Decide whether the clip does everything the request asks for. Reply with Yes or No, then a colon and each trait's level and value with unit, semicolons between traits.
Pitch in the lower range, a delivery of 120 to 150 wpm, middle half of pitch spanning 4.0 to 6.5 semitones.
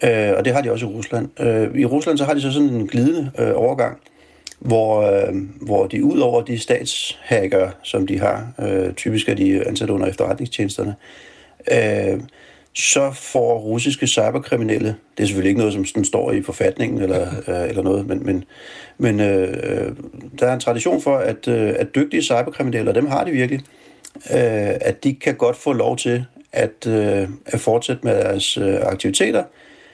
No: low, 115 Hz; average, 180 wpm; average, 4.7 semitones